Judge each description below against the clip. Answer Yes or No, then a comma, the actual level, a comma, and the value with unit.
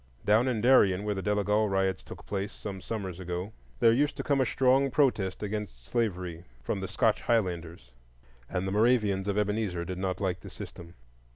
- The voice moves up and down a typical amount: Yes, average, 3.3 semitones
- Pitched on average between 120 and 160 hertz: No, low, 100 Hz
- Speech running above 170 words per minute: Yes, average, 185 wpm